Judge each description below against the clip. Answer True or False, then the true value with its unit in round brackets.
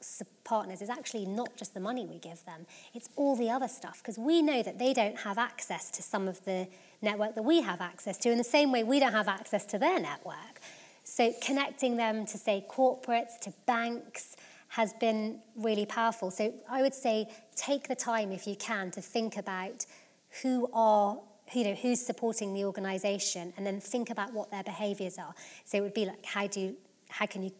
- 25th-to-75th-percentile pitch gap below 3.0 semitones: False (3.3 semitones)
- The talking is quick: True (210 wpm)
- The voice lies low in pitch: False (220 Hz)